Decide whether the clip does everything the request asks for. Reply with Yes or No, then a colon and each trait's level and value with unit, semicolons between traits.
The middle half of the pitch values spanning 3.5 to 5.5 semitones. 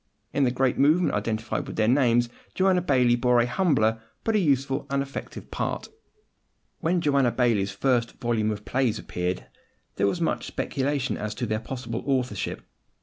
Yes: average, 3.8 semitones